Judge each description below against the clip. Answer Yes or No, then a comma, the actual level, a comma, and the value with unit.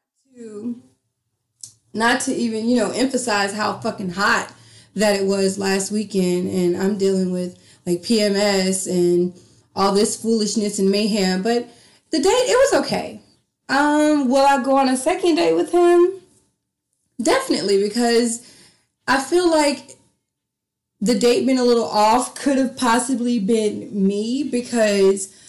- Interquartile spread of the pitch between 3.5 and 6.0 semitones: Yes, average, 4.9 semitones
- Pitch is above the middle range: Yes, high, 220 Hz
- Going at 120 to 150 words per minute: Yes, average, 140 wpm